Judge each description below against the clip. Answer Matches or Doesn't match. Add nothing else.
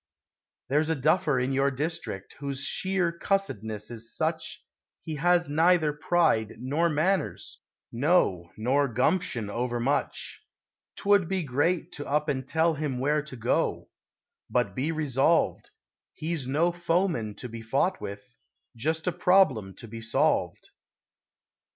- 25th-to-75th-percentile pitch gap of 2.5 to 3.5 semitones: Doesn't match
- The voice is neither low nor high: Matches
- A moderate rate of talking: Doesn't match